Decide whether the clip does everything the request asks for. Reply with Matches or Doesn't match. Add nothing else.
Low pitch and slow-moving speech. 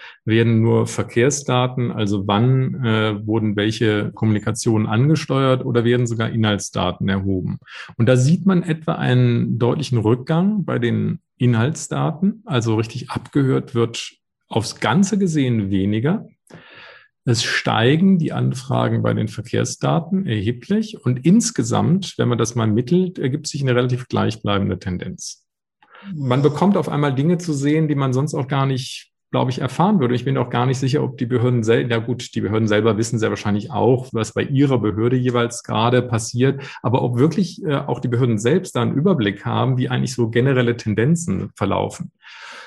Doesn't match